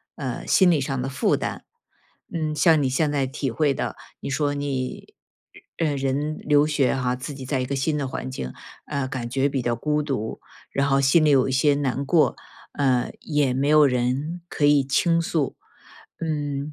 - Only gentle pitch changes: Yes, narrow, 2.1 semitones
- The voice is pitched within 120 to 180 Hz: Yes, medium, 140 Hz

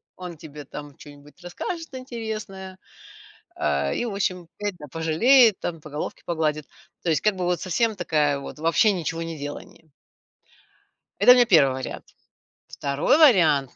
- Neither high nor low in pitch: Yes, medium, 170 Hz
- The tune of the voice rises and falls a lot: Yes, wide, 5.7 semitones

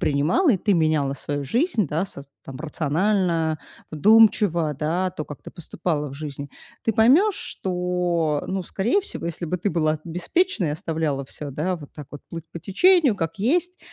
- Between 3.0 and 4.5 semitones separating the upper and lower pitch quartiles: No, average, 5.1 semitones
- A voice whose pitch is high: No, medium, 170 Hz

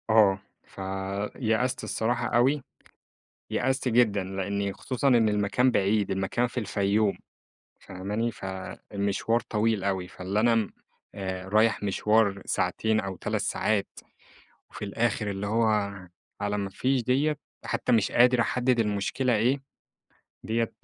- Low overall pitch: Yes, low, 105 Hz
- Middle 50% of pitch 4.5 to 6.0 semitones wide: No, average, 3.3 semitones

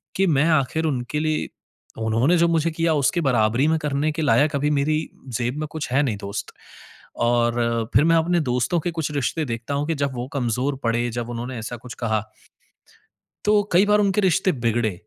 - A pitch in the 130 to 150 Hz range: Yes, medium, 140 Hz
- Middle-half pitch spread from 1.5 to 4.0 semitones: No, average, 5.0 semitones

